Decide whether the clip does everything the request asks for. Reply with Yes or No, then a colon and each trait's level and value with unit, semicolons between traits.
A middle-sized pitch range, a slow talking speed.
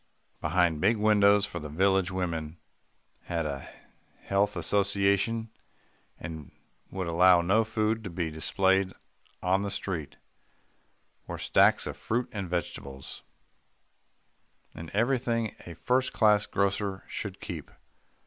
Yes: average, 3.5 semitones; slow, 120 wpm